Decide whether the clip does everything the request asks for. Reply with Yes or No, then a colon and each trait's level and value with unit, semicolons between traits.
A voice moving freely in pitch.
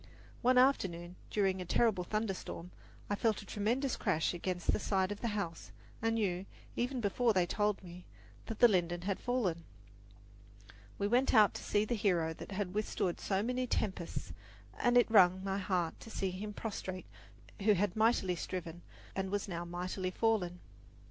No: average, 3.5 semitones